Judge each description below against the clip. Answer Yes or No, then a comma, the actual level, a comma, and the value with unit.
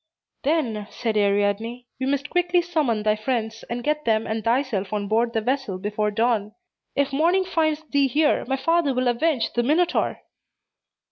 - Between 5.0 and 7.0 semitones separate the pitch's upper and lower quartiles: Yes, wide, 5.6 semitones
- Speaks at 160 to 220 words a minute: Yes, average, 165 wpm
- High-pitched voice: Yes, high, 245 Hz